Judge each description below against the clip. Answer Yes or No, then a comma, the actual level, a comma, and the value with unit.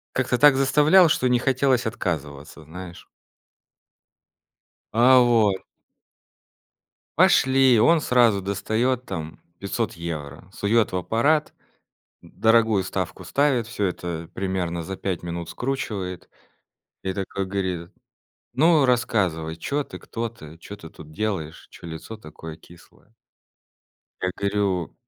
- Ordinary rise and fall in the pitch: No, wide, 6.1 semitones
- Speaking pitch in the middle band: No, low, 100 Hz